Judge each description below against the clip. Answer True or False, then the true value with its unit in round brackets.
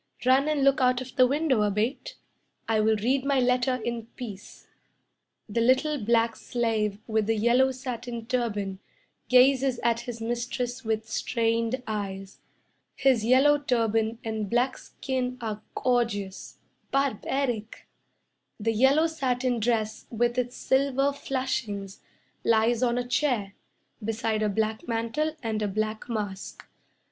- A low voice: False (235 Hz)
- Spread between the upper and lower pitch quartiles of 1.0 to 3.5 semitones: True (2.8 semitones)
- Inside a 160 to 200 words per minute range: False (135 wpm)